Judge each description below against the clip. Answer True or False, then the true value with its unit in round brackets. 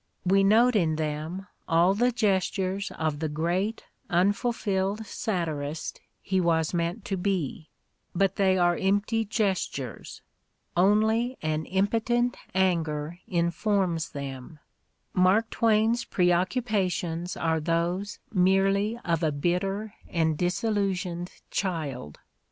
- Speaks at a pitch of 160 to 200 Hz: True (185 Hz)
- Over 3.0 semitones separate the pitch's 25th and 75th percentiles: True (3.6 semitones)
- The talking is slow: True (105 wpm)